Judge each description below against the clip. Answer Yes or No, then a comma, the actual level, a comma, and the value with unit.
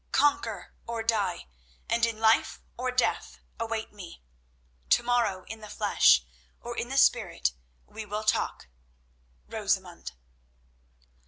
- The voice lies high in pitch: Yes, high, 215 Hz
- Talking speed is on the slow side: Yes, slow, 115 wpm